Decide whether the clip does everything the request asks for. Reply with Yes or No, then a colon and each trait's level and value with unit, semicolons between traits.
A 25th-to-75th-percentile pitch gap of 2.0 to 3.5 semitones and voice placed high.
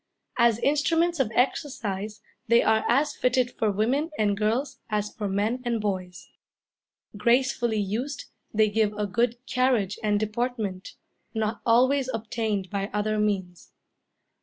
Yes: average, 3.2 semitones; high, 220 Hz